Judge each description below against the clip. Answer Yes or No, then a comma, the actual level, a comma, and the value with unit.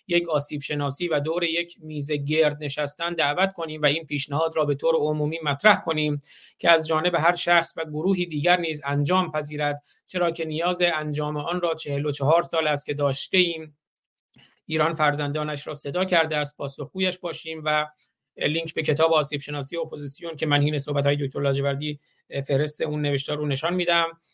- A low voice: No, medium, 155 Hz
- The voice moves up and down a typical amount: No, narrow, 2.3 semitones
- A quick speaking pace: Yes, fast, 180 wpm